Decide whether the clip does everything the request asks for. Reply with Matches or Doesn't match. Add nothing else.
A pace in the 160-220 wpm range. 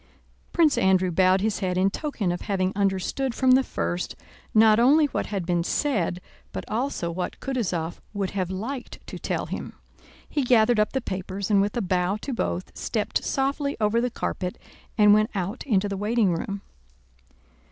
Matches